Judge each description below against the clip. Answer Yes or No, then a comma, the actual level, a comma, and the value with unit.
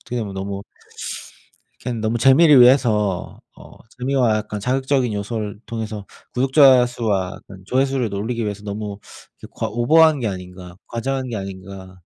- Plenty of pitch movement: No, average, 4.2 semitones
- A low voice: Yes, low, 110 Hz